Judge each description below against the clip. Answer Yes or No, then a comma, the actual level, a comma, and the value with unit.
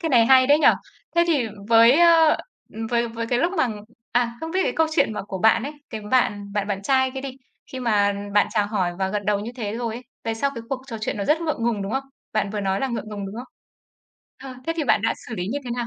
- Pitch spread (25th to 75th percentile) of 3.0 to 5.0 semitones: Yes, average, 4.3 semitones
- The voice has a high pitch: Yes, high, 235 Hz